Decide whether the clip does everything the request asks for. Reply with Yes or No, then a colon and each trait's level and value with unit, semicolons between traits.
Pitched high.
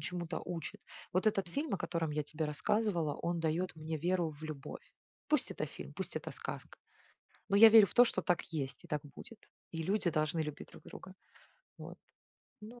No: medium, 170 Hz